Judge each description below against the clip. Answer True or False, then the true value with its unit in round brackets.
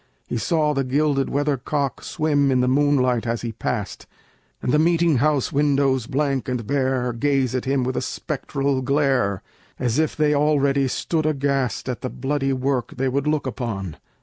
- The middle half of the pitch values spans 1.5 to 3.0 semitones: True (2.4 semitones)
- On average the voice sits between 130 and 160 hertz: True (135 Hz)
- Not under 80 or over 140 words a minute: False (175 wpm)